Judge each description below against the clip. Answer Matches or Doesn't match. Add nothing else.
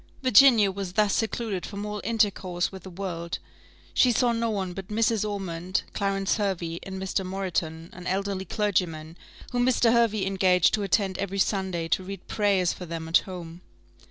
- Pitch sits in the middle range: Doesn't match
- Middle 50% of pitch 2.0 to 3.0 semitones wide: Matches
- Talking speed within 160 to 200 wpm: Matches